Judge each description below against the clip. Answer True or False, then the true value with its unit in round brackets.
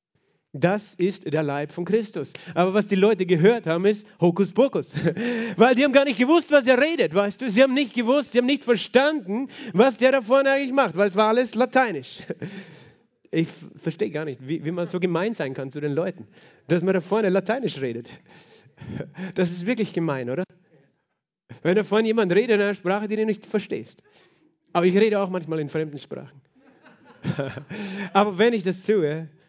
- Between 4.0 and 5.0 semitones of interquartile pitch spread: False (5.6 semitones)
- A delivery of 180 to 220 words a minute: True (190 wpm)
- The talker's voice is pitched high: True (195 Hz)